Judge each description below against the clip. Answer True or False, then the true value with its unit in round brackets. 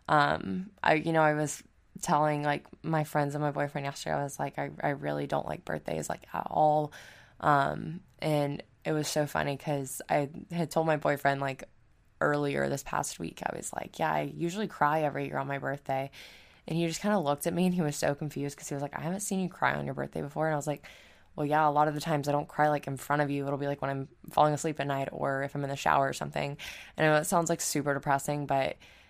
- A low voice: False (145 Hz)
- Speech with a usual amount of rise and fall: False (2.0 semitones)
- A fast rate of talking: True (260 wpm)